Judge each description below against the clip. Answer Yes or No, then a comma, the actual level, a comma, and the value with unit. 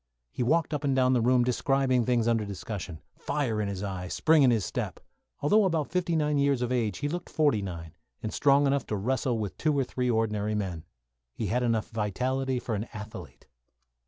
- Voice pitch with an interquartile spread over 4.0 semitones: Yes, average, 4.8 semitones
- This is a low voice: Yes, low, 125 Hz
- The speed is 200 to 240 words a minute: Yes, fast, 205 wpm